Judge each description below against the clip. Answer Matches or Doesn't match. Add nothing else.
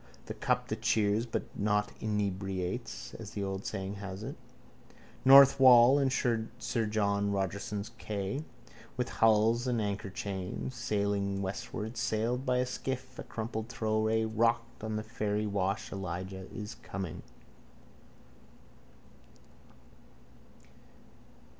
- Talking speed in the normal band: Doesn't match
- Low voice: Matches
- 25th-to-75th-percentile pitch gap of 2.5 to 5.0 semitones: Matches